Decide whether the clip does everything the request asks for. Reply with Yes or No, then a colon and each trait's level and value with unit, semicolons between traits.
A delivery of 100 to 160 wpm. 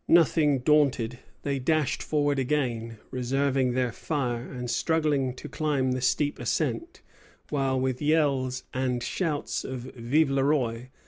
Yes: slow, 135 wpm